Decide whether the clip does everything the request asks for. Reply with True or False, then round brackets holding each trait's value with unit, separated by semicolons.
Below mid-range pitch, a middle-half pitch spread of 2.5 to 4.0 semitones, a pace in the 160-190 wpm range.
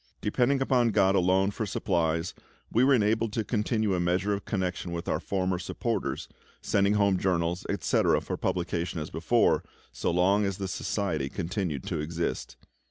True (95 Hz; 3.3 semitones; 165 wpm)